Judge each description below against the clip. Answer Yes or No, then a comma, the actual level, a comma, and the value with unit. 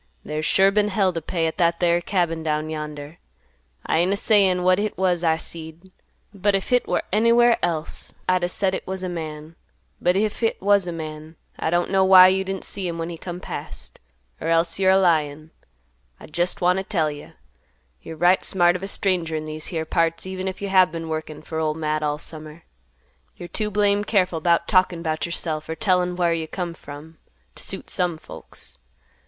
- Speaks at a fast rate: Yes, fast, 210 wpm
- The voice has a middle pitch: Yes, medium, 175 Hz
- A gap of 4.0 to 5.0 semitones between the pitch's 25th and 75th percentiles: No, average, 3.0 semitones